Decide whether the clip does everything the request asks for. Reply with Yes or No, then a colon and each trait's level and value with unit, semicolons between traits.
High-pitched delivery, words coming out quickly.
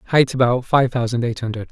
No: low, 125 Hz; fast, 210 wpm